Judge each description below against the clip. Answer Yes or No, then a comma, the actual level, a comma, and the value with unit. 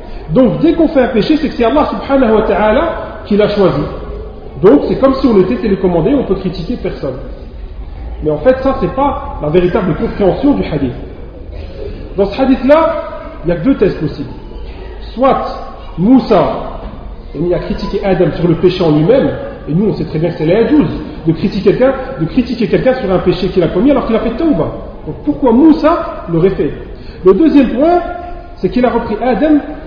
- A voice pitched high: Yes, high, 220 Hz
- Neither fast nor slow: Yes, average, 195 wpm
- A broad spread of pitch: Yes, wide, 7.1 semitones